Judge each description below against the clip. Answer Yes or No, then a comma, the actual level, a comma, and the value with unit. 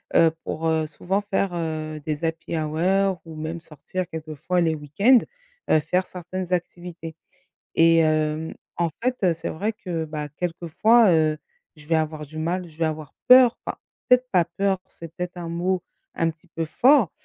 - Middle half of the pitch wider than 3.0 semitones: No, average, 2.7 semitones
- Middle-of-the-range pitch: Yes, medium, 165 Hz